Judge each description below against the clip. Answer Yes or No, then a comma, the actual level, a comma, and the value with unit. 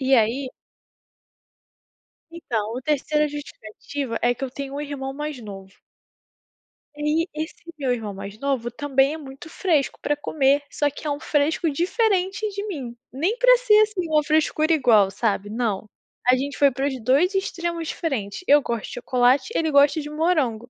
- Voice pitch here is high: Yes, very high, 285 Hz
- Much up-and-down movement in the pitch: No, average, 4.4 semitones